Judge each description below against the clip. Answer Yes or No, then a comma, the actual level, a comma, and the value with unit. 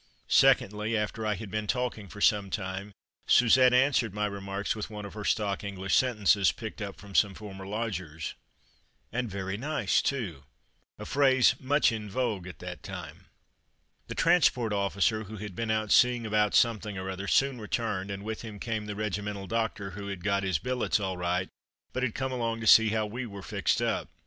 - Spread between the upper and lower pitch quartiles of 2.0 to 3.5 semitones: Yes, average, 2.7 semitones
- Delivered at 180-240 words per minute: Yes, average, 190 wpm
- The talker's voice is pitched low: Yes, low, 105 Hz